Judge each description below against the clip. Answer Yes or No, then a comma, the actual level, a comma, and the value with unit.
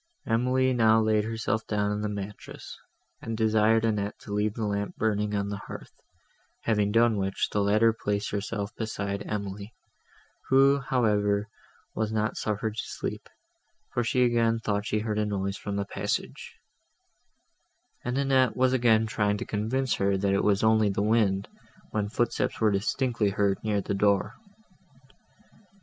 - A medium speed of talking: Yes, average, 160 wpm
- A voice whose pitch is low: Yes, low, 105 Hz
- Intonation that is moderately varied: No, narrow, 1.8 semitones